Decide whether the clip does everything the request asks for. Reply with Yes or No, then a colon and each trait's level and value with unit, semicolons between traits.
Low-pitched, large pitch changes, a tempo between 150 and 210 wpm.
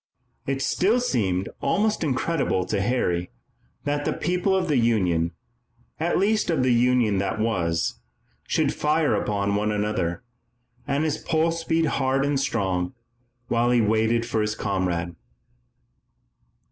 No: low, 120 Hz; wide, 7.3 semitones; slow, 135 wpm